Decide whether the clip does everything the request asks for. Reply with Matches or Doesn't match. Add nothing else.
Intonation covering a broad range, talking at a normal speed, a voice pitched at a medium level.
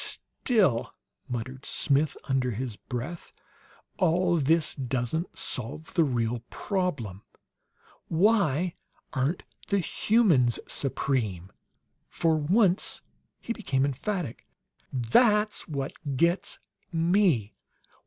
Doesn't match